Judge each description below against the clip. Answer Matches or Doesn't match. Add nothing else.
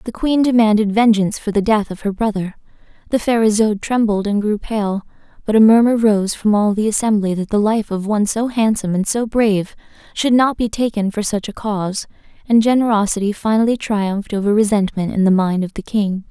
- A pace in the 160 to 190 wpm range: Doesn't match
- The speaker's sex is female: Matches